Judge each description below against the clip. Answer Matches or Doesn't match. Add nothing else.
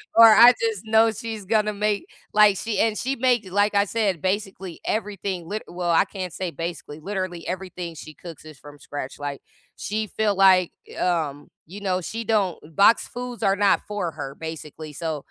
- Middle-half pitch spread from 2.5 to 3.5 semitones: Doesn't match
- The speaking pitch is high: Matches